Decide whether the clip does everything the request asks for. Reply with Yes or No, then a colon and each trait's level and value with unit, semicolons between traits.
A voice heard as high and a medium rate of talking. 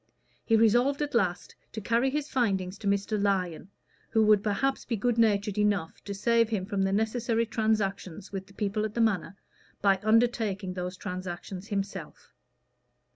Yes: high, 210 Hz; average, 165 wpm